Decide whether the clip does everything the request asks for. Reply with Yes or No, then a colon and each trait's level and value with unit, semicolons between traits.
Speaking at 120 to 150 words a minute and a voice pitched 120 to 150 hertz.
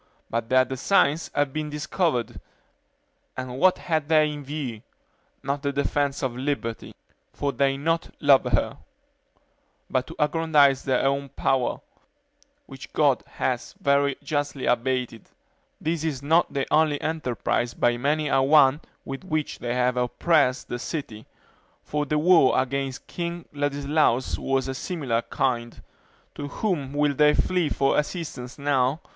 Yes: average, 145 wpm; medium, 140 Hz